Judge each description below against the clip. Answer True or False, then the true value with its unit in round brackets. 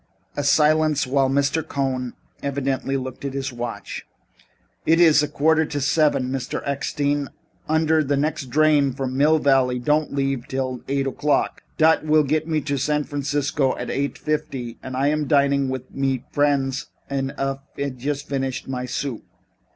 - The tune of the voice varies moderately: False (1.9 semitones)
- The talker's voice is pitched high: False (140 Hz)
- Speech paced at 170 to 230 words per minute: False (160 wpm)